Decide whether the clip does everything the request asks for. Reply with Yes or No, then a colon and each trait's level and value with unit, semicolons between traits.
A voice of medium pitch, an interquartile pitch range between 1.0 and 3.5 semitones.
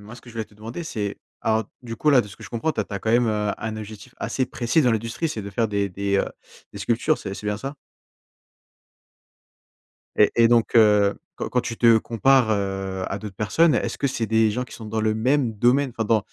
No: low, 110 Hz; average, 2.8 semitones